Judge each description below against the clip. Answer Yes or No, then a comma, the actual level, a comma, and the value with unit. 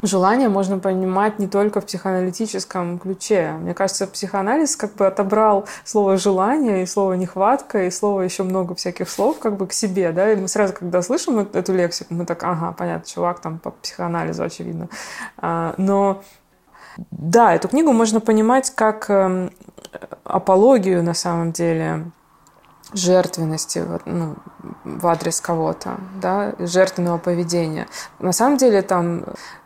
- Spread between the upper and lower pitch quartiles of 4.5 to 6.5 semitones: No, average, 2.8 semitones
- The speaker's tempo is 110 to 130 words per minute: No, average, 140 wpm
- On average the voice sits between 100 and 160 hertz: No, high, 190 Hz